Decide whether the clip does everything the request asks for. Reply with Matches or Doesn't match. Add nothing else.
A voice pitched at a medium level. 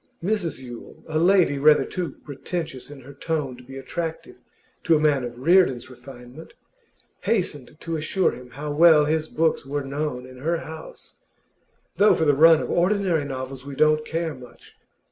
Matches